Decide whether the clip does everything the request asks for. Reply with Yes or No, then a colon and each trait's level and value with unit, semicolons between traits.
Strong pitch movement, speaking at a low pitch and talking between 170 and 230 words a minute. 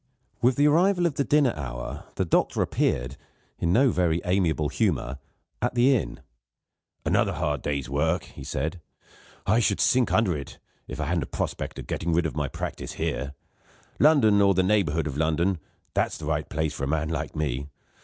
Yes: wide, 6.7 semitones; very low, 85 Hz; average, 185 wpm